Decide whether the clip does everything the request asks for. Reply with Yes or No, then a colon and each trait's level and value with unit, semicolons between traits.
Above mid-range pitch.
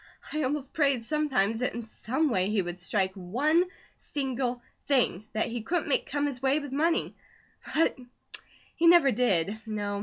Yes: very high, 255 Hz